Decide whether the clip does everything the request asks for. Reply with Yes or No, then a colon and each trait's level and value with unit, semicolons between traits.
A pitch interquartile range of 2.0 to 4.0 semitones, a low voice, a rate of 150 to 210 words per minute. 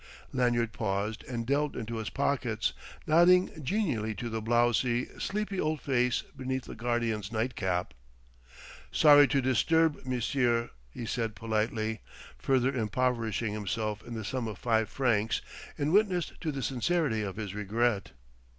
No: average, 3.6 semitones; low, 120 Hz; average, 140 wpm